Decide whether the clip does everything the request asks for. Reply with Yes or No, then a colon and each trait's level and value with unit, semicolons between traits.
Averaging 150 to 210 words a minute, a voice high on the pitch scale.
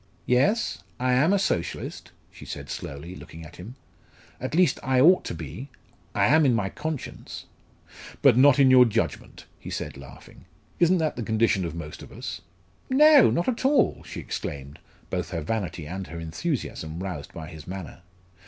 No: average, 175 wpm; low, 110 Hz